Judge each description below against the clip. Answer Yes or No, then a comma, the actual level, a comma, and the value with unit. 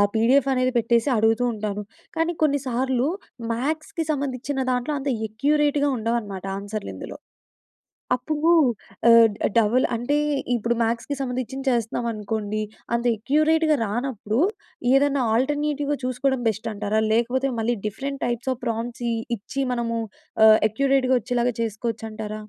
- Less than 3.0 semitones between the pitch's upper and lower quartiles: No, average, 3.7 semitones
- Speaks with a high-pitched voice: Yes, high, 245 Hz